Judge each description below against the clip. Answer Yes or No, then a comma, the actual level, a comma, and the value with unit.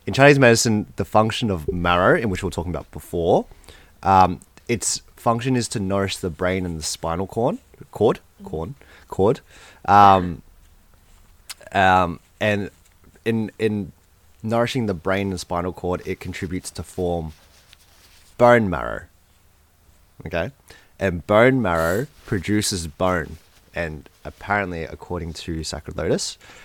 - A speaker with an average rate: No, slow, 130 wpm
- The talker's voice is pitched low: Yes, very low, 90 Hz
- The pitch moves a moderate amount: Yes, average, 3.5 semitones